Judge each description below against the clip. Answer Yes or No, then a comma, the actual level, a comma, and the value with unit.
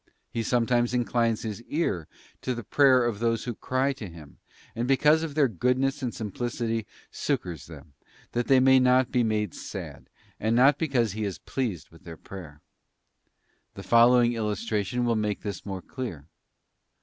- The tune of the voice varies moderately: Yes, average, 3.6 semitones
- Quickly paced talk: No, average, 165 wpm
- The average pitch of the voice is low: Yes, low, 115 Hz